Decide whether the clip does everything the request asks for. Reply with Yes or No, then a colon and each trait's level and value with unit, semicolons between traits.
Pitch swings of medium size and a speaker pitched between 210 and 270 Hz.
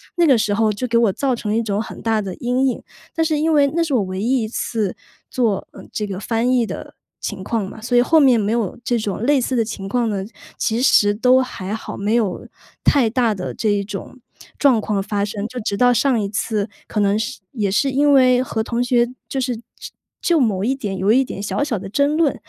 Yes: average, 3.7 semitones; high, 230 Hz